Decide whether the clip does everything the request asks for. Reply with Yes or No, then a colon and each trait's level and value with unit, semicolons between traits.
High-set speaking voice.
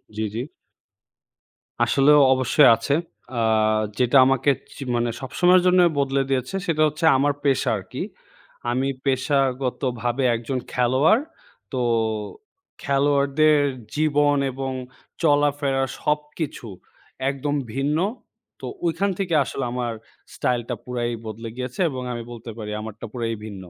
No: low, 135 Hz